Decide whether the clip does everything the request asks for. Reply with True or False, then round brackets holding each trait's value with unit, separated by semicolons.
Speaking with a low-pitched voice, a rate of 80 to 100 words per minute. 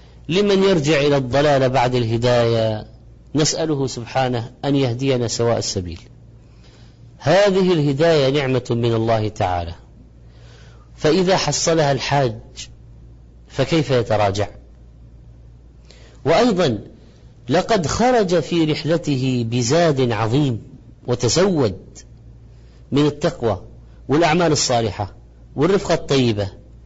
True (120 Hz; 85 wpm)